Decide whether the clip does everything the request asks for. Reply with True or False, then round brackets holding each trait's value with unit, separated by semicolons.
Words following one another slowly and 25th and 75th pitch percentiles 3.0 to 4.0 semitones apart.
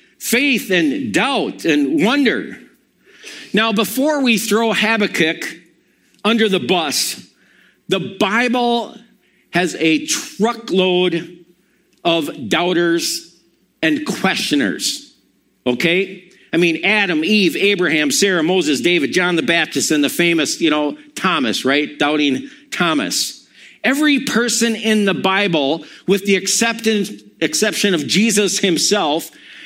False (110 wpm; 5.3 semitones)